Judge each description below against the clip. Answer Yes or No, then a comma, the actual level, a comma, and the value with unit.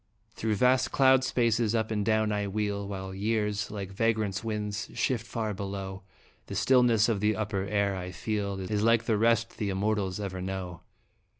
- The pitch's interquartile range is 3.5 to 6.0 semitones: No, narrow, 2.4 semitones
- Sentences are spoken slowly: No, average, 175 wpm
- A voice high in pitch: No, low, 105 Hz